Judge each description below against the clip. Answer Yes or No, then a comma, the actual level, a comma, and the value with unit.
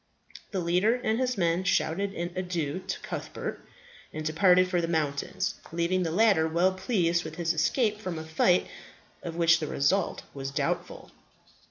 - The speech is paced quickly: No, average, 165 wpm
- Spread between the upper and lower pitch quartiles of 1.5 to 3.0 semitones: Yes, average, 2.7 semitones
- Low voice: No, medium, 175 Hz